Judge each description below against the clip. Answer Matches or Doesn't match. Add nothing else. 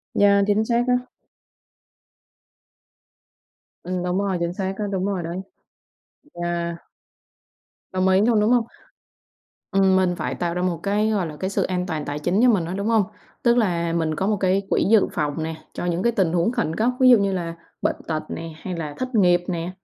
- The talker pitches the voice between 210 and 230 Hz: Doesn't match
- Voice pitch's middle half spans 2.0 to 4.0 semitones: Matches